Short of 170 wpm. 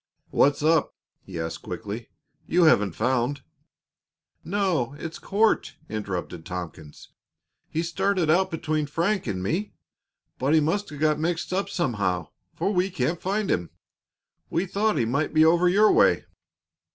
Yes: average, 150 wpm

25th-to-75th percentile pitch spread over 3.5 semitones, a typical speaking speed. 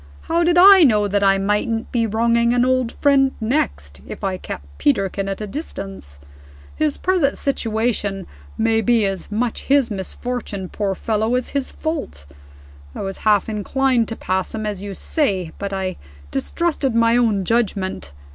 Yes: average, 4.2 semitones; average, 165 wpm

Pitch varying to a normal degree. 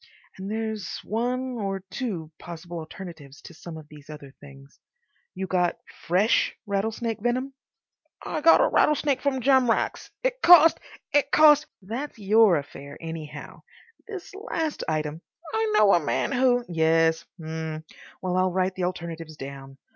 No: wide, 7.4 semitones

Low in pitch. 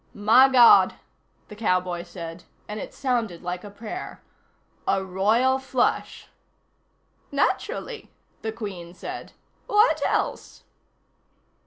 No: high, 210 Hz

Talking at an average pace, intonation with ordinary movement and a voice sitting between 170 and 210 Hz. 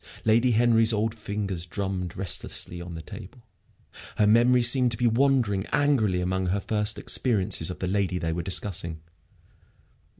No: average, 155 wpm; average, 4.1 semitones; low, 100 Hz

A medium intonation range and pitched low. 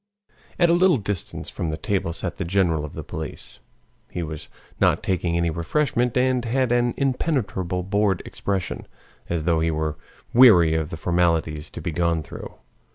No: wide, 6.6 semitones; very low, 90 Hz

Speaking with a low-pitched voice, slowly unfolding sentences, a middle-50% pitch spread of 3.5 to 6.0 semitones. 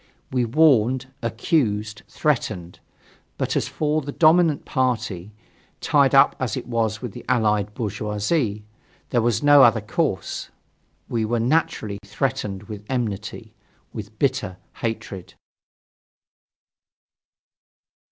Yes: low, 115 Hz; slow, 110 wpm; average, 4.0 semitones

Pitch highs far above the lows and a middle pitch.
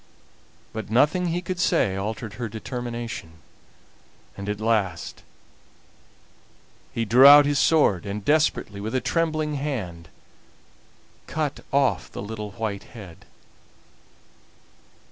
No: wide, 6.1 semitones; low, 115 Hz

